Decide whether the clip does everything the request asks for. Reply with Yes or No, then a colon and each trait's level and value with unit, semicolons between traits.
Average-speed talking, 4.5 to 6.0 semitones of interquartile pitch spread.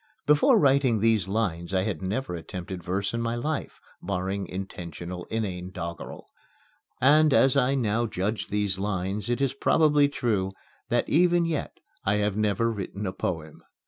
Yes: average, 155 wpm; average, 5.2 semitones